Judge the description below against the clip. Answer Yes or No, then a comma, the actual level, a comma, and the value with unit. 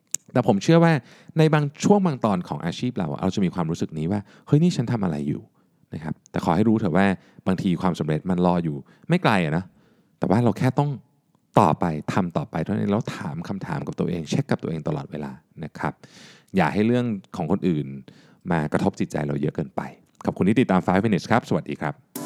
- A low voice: Yes, low, 115 Hz